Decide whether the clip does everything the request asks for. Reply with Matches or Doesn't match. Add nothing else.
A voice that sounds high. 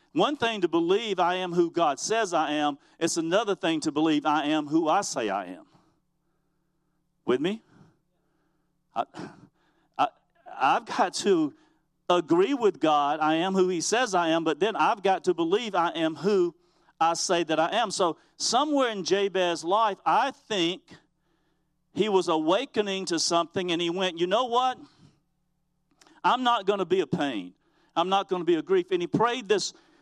Doesn't match